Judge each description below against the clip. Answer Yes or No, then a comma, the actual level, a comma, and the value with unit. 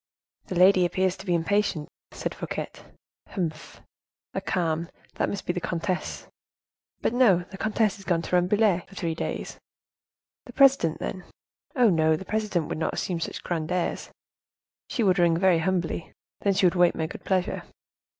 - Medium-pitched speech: Yes, medium, 180 Hz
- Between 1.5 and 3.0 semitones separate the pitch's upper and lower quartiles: Yes, average, 2.7 semitones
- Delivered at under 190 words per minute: Yes, average, 170 wpm